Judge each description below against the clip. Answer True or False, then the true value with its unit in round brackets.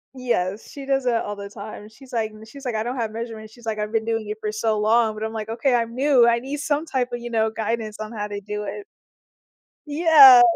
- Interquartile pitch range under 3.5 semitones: True (2.6 semitones)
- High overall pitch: True (225 Hz)